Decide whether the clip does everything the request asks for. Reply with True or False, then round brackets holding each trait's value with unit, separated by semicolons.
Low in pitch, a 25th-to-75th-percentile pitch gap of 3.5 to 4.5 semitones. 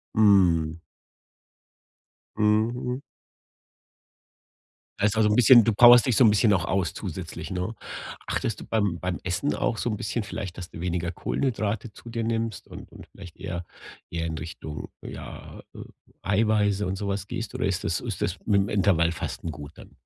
True (100 Hz; 4.1 semitones)